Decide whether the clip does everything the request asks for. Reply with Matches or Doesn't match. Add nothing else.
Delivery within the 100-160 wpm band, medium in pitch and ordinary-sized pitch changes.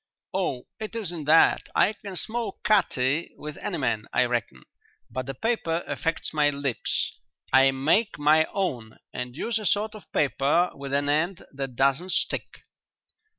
Doesn't match